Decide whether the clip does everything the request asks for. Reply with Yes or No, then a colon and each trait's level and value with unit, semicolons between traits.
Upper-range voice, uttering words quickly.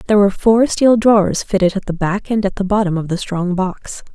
Yes: high, 200 Hz; fast, 245 wpm